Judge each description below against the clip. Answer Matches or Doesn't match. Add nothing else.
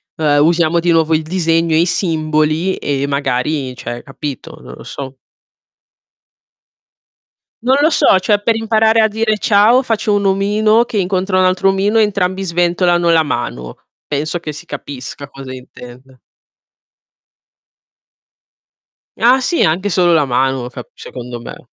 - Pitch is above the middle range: Doesn't match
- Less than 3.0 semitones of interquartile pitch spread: Doesn't match